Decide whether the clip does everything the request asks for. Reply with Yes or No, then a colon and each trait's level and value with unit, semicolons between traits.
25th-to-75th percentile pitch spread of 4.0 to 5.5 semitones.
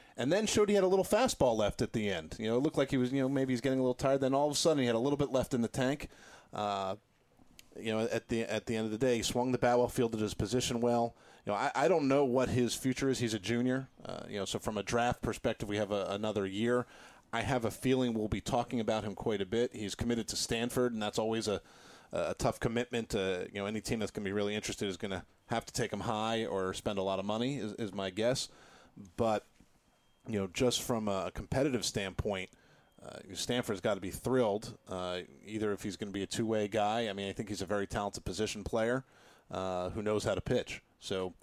No: average, 3.3 semitones